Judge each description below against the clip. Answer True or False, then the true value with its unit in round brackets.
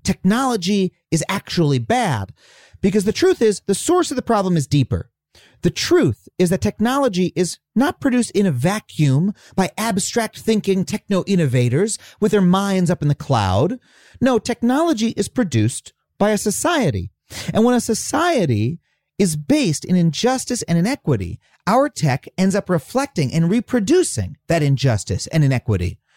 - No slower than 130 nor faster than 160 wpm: True (150 wpm)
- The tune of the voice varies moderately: False (7.1 semitones)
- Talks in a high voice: True (195 Hz)